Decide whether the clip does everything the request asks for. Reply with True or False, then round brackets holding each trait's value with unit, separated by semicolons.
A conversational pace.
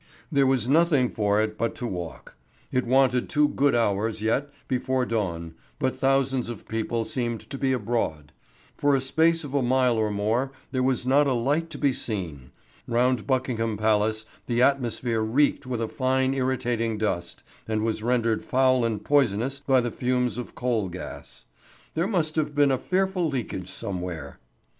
True (170 wpm)